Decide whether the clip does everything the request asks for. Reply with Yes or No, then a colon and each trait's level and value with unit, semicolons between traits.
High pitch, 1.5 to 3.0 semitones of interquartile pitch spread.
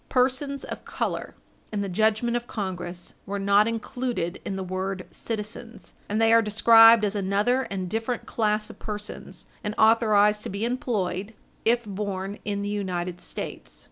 Yes: high, 210 Hz; narrow, 2.6 semitones